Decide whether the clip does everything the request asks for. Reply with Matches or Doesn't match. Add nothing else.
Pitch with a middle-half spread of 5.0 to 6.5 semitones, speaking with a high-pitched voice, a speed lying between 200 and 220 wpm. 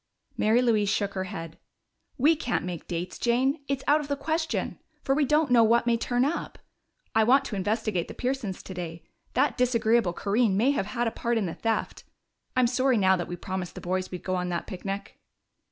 Matches